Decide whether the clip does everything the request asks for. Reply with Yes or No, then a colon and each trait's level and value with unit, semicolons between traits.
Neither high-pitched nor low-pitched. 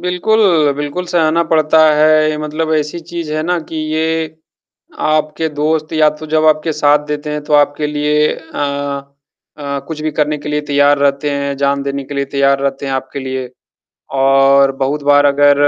Yes: medium, 150 Hz